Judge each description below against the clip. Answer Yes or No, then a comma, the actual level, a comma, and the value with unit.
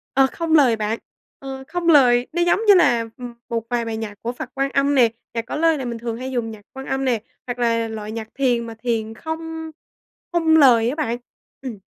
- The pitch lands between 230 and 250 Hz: Yes, high, 245 Hz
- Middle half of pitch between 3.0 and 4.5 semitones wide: Yes, average, 3.9 semitones